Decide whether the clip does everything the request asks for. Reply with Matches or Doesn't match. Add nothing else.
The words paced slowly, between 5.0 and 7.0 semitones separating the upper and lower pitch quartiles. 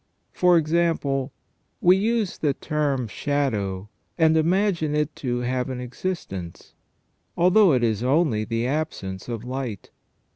Matches